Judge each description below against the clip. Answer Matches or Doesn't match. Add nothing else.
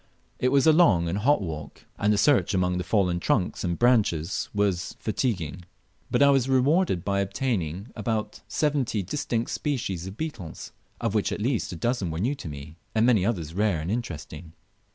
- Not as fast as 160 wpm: Doesn't match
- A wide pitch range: Matches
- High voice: Doesn't match